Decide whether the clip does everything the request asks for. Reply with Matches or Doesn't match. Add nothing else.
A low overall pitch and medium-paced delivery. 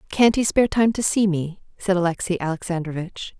Doesn't match